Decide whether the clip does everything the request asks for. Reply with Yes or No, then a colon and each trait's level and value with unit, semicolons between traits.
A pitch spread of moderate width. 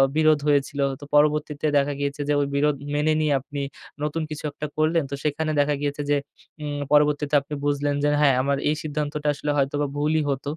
No: narrow, 1.0 semitones